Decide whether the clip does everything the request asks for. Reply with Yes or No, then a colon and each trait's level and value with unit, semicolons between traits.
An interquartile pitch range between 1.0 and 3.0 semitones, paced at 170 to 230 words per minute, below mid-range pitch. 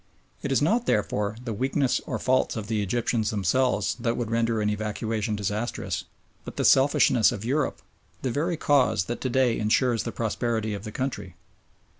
No: average, 3.5 semitones; average, 175 wpm; low, 115 Hz